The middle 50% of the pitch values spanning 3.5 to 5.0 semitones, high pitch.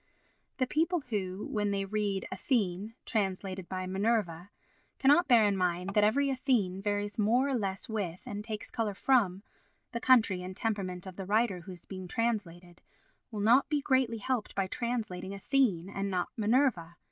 Yes: average, 3.9 semitones; high, 205 Hz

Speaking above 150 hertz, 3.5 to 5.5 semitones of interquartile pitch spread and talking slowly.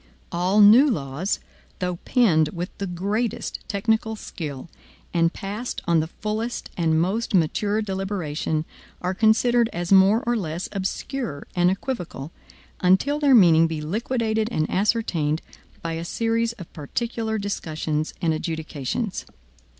Yes: high, 190 Hz; average, 5.2 semitones; slow, 130 wpm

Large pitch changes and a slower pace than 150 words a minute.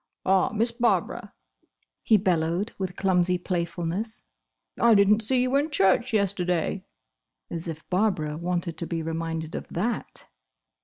No: average, 4.3 semitones; slow, 135 wpm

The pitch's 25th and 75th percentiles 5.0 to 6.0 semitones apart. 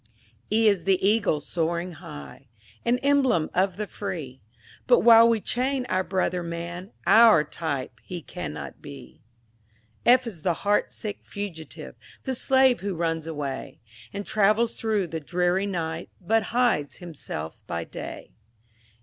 Yes: wide, 5.4 semitones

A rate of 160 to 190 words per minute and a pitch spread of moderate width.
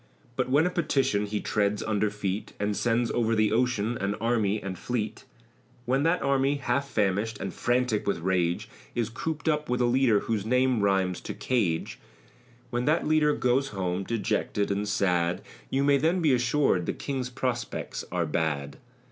Yes: average, 175 wpm; average, 4.7 semitones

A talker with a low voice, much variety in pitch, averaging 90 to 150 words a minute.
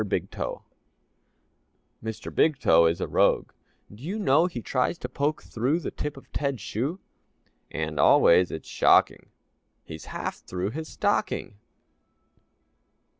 Yes: low, 125 Hz; wide, 7.8 semitones; slow, 135 wpm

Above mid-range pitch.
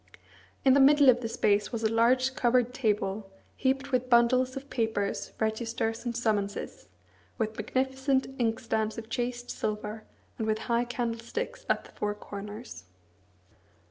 Yes: high, 235 Hz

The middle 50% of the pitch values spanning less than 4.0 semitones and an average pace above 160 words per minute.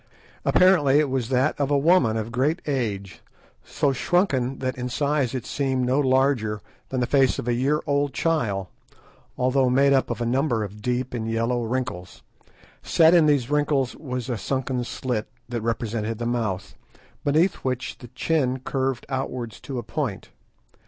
Yes: average, 3.0 semitones; average, 170 wpm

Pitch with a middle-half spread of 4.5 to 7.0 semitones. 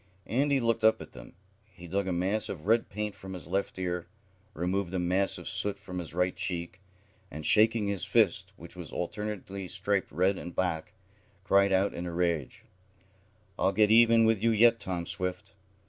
No: average, 3.1 semitones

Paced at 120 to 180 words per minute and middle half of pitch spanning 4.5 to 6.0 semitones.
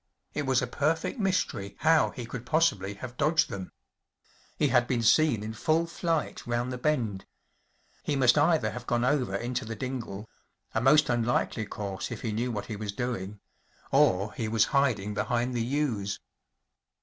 Yes: average, 175 wpm; average, 4.9 semitones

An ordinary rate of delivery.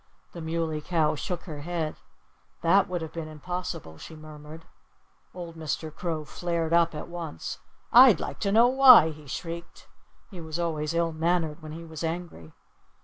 Yes: average, 165 wpm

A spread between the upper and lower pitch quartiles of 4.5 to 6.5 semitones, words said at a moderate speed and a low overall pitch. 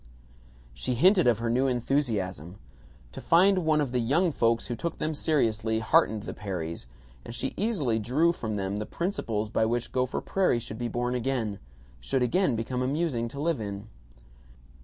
Yes: wide, 5.5 semitones; average, 175 wpm; low, 120 Hz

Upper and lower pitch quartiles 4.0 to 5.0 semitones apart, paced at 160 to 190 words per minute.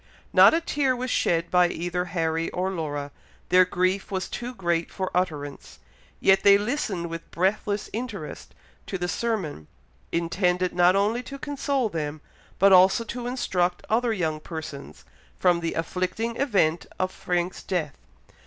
No: average, 4.3 semitones; average, 150 wpm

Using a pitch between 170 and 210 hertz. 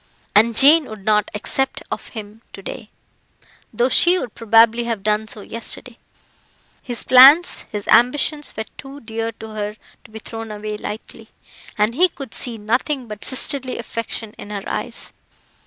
No: high, 225 Hz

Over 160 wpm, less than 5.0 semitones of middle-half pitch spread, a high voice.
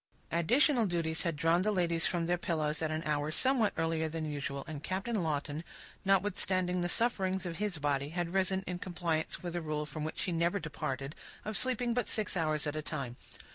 No: average, 200 wpm; average, 3.5 semitones; medium, 170 Hz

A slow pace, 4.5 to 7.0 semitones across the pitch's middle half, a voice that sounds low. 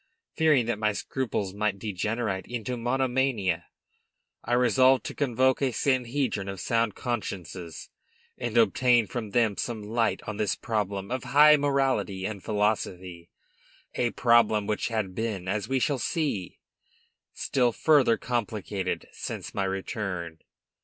No: slow, 130 wpm; average, 3.9 semitones; low, 110 Hz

